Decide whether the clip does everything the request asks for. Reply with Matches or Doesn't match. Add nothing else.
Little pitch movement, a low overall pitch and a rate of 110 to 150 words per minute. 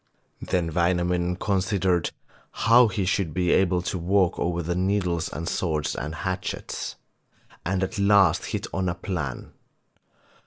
Matches